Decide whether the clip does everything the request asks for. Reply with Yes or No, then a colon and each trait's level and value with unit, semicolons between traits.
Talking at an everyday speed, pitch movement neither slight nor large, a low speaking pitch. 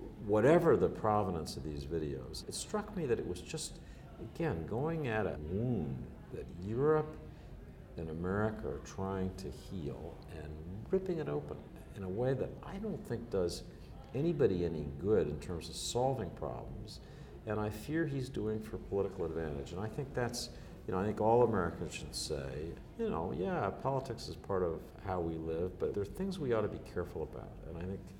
No: average, 190 wpm; wide, 7.0 semitones; very low, 95 Hz